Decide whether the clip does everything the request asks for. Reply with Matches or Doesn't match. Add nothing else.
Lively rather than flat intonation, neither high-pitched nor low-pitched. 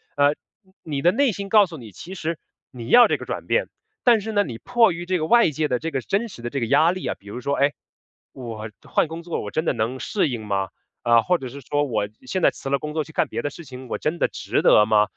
Matches